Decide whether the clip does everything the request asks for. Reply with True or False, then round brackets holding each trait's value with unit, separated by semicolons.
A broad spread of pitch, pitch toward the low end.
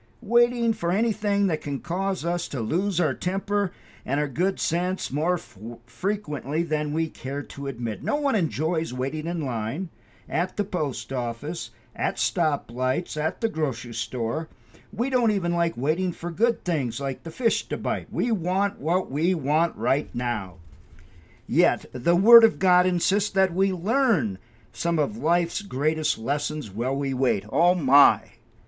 False (6.4 semitones; 165 Hz)